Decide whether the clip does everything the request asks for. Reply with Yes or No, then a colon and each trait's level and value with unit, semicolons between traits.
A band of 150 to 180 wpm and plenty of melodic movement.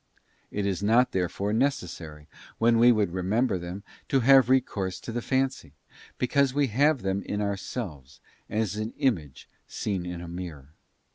Yes: average, 155 wpm; wide, 5.8 semitones